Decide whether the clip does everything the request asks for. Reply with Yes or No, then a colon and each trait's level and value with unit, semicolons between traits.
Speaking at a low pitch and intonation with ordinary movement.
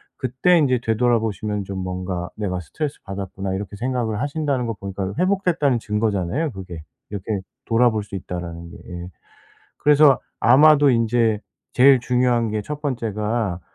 Yes: low, 110 Hz; average, 4.8 semitones